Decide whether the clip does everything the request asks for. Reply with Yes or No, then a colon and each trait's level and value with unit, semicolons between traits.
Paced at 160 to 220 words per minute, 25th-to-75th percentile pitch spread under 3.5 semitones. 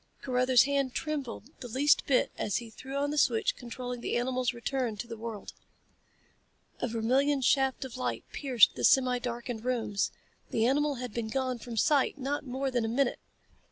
Yes: average, 180 wpm; narrow, 2.5 semitones